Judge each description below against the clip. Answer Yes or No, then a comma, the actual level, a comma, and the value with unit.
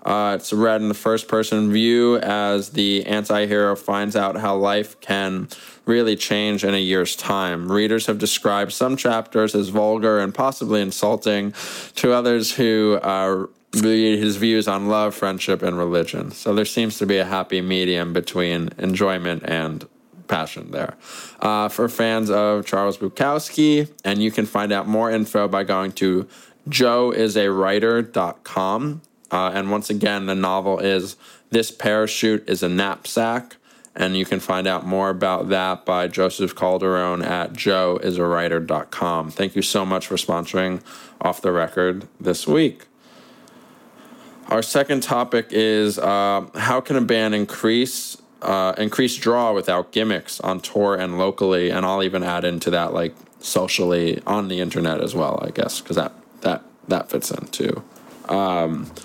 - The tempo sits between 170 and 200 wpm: No, average, 155 wpm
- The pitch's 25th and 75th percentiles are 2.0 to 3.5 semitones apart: Yes, average, 2.8 semitones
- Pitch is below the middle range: Yes, low, 100 Hz